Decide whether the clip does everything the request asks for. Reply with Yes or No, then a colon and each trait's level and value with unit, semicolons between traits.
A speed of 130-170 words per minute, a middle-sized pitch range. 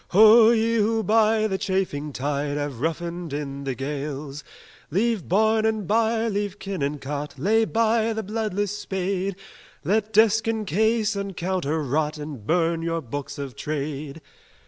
No: average, 155 wpm; wide, 6.7 semitones